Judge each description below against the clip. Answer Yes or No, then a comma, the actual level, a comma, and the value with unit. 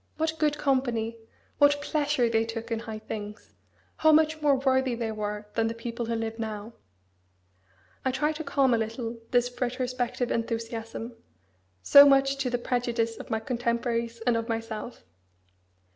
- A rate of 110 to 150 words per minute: No, average, 160 wpm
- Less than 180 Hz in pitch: No, high, 235 Hz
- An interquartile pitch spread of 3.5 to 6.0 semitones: No, average, 2.8 semitones